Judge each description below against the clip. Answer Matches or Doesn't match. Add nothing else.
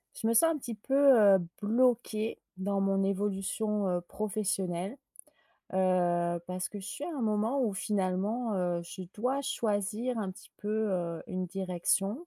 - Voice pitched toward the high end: Matches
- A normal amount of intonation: Matches